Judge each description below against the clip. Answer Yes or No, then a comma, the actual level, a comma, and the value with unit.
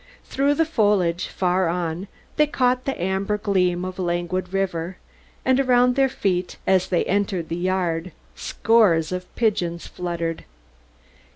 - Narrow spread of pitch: No, average, 3.9 semitones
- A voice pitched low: No, medium, 185 Hz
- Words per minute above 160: No, average, 145 wpm